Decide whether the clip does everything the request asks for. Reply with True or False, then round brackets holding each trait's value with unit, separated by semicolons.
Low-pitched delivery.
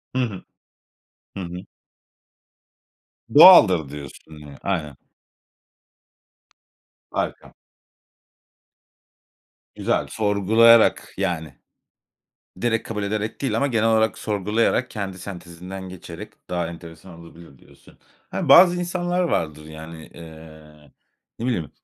True (95 Hz)